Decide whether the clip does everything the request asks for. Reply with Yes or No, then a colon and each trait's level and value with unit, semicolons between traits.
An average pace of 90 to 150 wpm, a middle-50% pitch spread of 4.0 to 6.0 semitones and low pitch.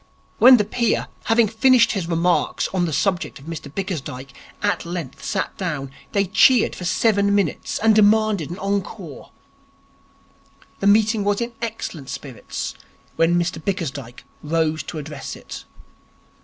No: average, 140 wpm; average, 5.1 semitones; medium, 185 Hz